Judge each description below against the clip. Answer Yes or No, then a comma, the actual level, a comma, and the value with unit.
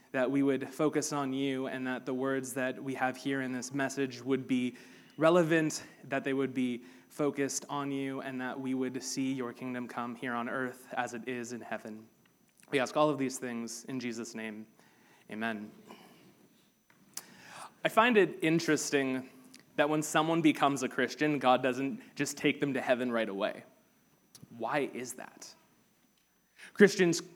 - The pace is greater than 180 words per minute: No, average, 165 wpm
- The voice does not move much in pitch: Yes, narrow, 2.0 semitones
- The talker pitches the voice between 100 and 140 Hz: Yes, low, 130 Hz